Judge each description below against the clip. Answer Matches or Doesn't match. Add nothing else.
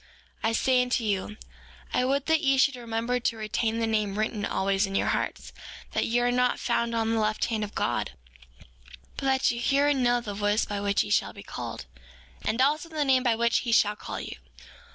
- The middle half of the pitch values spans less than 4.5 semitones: Matches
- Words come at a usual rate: Doesn't match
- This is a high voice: Matches